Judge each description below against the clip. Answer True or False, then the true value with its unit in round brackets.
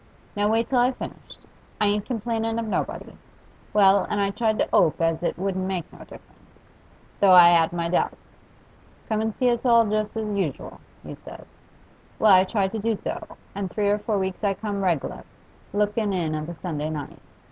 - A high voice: True (200 Hz)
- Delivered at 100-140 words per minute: False (195 wpm)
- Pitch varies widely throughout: False (3.2 semitones)